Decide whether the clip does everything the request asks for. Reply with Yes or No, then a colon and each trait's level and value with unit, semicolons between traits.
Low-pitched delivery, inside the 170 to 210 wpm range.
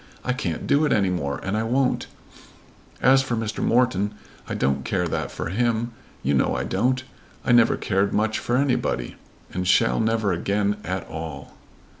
Yes: low, 105 Hz; average, 180 wpm